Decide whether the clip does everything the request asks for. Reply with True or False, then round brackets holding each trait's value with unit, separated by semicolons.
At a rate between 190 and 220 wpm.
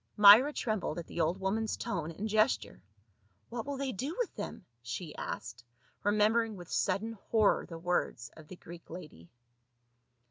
False (165 wpm)